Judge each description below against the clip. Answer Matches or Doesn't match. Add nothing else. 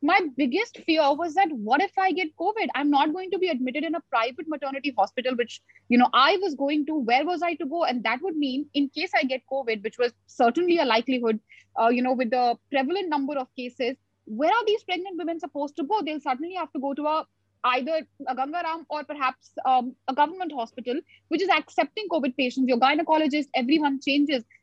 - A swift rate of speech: Matches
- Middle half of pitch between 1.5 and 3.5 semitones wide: Doesn't match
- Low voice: Doesn't match